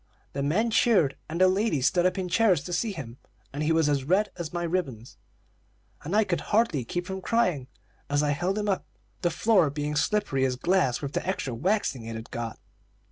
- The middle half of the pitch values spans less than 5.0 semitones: No, wide, 5.4 semitones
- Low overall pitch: No, medium, 170 Hz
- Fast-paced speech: Yes, fast, 210 wpm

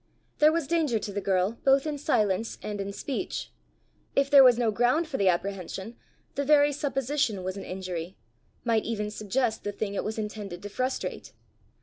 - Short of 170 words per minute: No, average, 185 wpm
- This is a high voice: Yes, high, 220 Hz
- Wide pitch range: Yes, wide, 5.7 semitones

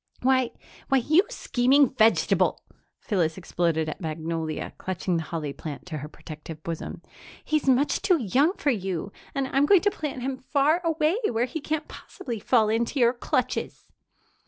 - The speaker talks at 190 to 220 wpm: No, average, 160 wpm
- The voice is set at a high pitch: Yes, high, 240 Hz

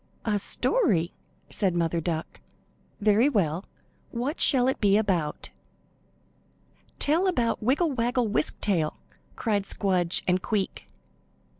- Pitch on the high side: Yes, high, 205 Hz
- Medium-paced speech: No, slow, 115 wpm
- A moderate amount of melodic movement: No, wide, 5.7 semitones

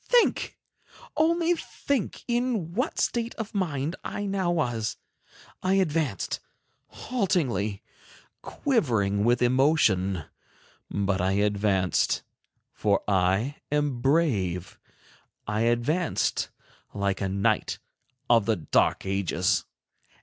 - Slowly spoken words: Yes, slow, 100 wpm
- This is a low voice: Yes, low, 120 Hz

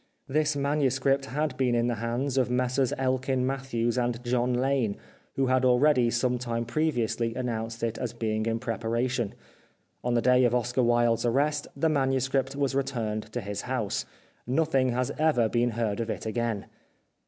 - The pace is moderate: Yes, average, 170 wpm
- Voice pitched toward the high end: No, low, 125 Hz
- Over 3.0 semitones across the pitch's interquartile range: No, narrow, 2.4 semitones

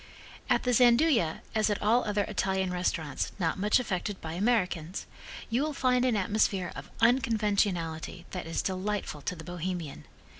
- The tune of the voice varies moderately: Yes, average, 4.3 semitones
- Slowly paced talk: No, average, 155 wpm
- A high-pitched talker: Yes, high, 200 Hz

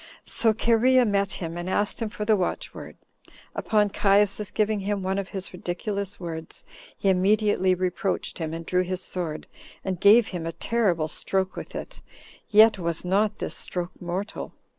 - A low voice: No, high, 195 Hz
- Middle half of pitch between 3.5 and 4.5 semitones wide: No, average, 2.7 semitones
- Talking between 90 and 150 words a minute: No, average, 165 wpm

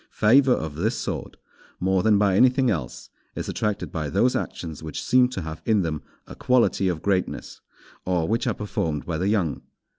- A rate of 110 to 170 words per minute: No, average, 185 wpm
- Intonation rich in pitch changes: Yes, wide, 5.7 semitones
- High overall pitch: No, very low, 95 Hz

